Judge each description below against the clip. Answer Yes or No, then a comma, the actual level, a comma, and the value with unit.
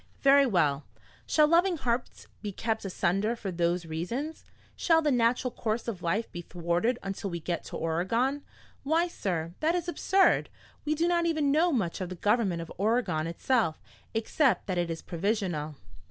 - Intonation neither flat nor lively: No, wide, 8.4 semitones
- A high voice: Yes, high, 220 Hz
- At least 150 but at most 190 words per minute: Yes, average, 170 wpm